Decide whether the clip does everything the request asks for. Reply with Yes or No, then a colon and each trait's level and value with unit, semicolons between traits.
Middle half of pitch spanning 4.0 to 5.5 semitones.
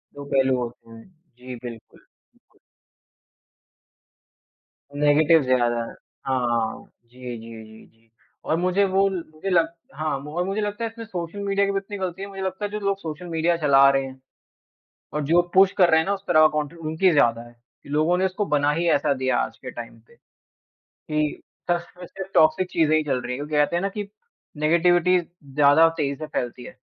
Yes: average, 5.2 semitones